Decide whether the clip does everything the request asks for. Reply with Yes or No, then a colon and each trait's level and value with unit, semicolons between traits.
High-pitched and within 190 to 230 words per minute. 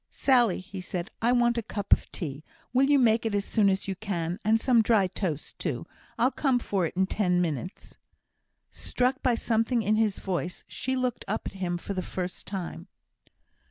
Yes: high, 205 Hz; average, 195 wpm